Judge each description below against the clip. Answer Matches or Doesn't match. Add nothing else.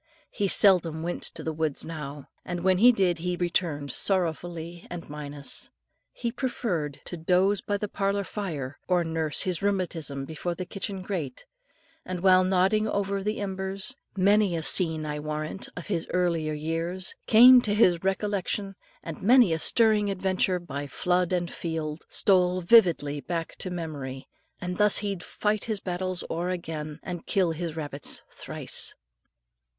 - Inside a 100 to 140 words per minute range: Doesn't match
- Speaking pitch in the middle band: Matches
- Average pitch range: Matches